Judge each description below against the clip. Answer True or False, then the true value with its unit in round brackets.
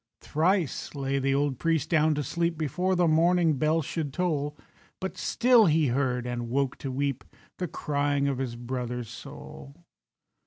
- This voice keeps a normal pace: True (155 wpm)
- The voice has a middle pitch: True (145 Hz)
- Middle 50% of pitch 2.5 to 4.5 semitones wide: True (3.8 semitones)